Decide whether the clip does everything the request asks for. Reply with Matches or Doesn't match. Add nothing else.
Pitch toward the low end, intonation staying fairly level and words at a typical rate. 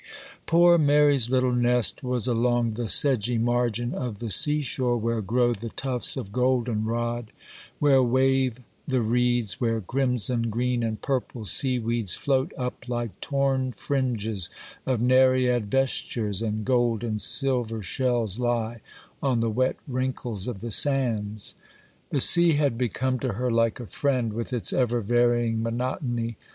Matches